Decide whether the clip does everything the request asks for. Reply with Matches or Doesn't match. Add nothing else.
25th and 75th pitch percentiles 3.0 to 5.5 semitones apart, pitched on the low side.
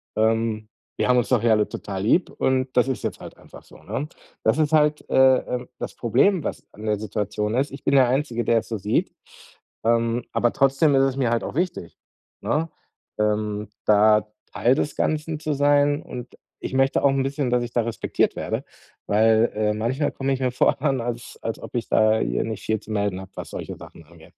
Matches